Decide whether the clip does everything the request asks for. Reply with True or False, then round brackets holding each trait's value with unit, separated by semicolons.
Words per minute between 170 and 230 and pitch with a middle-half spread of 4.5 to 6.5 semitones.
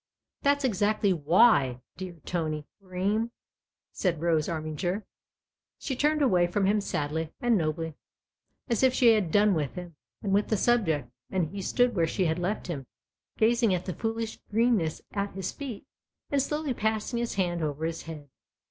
True (175 wpm; 5.6 semitones)